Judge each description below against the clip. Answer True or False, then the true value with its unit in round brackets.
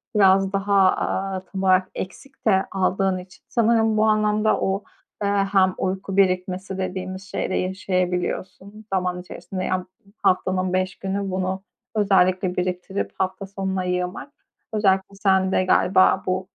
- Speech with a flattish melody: True (1.1 semitones)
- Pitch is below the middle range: False (190 Hz)